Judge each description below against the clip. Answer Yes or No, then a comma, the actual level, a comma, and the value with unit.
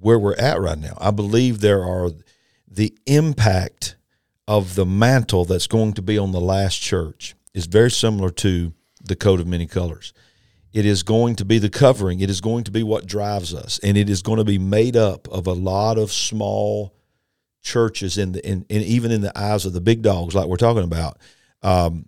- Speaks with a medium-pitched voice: No, low, 100 Hz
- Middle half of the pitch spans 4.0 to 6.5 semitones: No, average, 3.0 semitones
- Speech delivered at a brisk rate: Yes, fast, 210 wpm